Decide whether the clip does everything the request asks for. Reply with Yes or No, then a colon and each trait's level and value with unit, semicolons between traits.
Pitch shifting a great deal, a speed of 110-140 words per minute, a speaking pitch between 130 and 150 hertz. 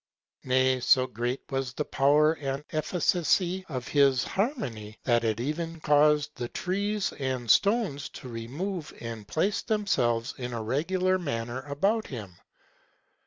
Yes: wide, 6.2 semitones; slow, 135 wpm; medium, 140 Hz